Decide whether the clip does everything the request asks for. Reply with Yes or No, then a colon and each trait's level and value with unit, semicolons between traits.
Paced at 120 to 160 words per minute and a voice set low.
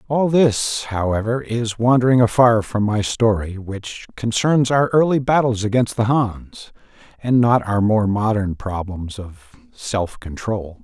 Yes: average, 145 wpm; low, 110 Hz